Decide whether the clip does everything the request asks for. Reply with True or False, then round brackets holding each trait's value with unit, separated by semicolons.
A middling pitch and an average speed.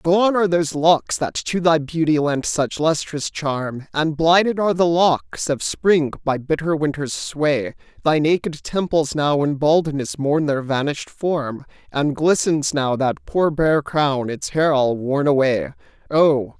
True (150 Hz; 165 wpm)